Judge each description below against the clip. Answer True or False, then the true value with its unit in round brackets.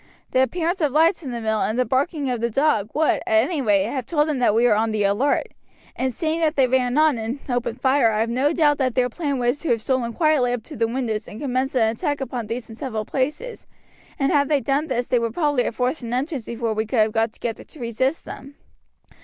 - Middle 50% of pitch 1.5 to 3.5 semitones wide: False (4.1 semitones)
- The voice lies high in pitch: True (255 Hz)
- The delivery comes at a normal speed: False (255 wpm)